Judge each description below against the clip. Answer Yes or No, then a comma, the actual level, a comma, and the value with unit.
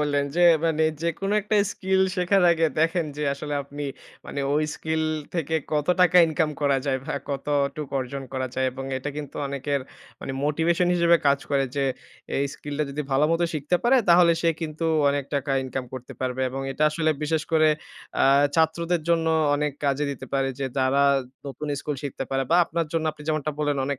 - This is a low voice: No, medium, 150 Hz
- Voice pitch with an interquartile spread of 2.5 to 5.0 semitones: Yes, average, 2.8 semitones